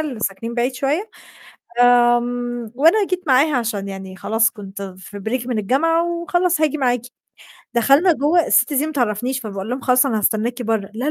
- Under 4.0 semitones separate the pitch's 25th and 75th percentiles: No, average, 5.0 semitones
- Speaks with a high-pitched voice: Yes, high, 245 Hz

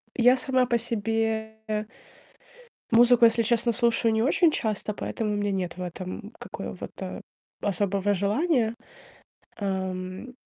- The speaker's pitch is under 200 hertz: No, high, 220 Hz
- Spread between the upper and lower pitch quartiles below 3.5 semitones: Yes, average, 2.9 semitones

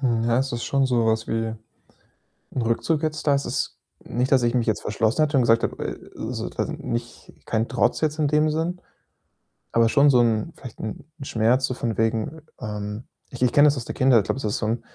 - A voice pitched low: Yes, low, 120 Hz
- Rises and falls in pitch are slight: No, average, 3.7 semitones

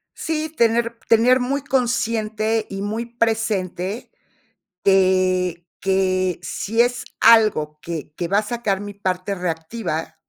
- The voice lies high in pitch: Yes, high, 205 Hz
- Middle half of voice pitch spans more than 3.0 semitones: Yes, average, 4.0 semitones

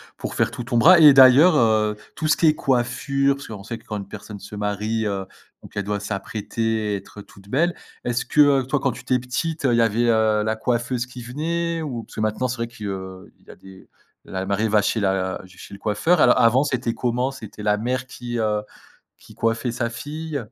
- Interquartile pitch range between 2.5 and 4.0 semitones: Yes, average, 3.7 semitones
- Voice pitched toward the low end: Yes, low, 115 Hz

